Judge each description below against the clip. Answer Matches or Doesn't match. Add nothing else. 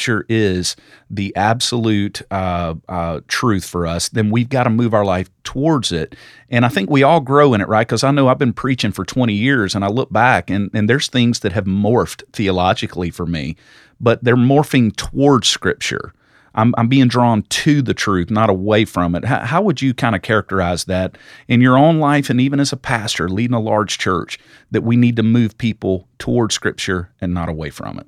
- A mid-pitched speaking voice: Doesn't match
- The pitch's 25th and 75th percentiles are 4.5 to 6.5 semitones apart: Matches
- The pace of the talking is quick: Matches